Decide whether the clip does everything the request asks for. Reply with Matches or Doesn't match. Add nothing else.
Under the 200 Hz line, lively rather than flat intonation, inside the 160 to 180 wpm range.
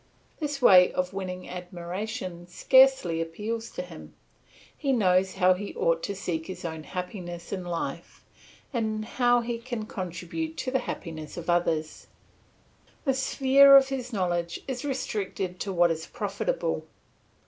Doesn't match